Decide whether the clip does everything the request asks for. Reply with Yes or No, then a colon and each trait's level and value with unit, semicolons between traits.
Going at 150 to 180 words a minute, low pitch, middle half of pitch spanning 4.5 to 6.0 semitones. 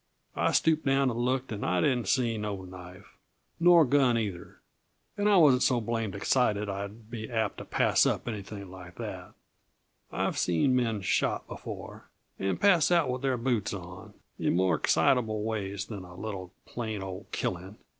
Yes: average, 170 wpm; low, 110 Hz; average, 4.8 semitones